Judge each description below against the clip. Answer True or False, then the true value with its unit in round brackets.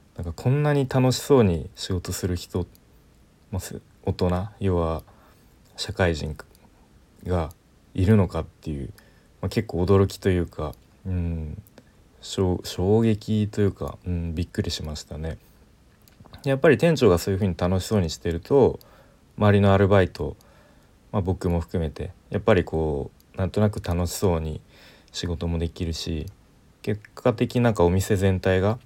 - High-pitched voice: False (95 Hz)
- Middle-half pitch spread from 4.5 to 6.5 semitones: False (3.8 semitones)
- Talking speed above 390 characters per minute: False (245 characters per minute)